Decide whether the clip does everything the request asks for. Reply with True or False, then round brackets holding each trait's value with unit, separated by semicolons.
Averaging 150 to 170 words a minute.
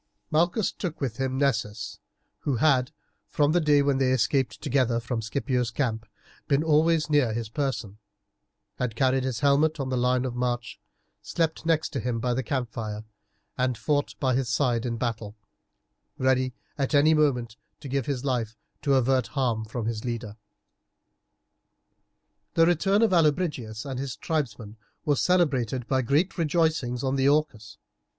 True (160 wpm)